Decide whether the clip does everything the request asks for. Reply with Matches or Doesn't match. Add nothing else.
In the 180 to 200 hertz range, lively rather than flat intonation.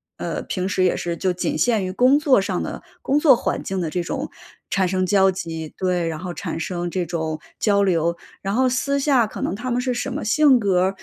Matches